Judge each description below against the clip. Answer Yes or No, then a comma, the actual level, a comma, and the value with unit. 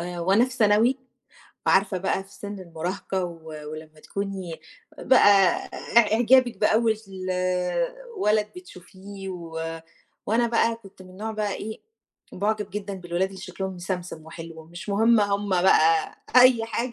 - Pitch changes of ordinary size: Yes, average, 3.6 semitones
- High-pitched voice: Yes, high, 195 Hz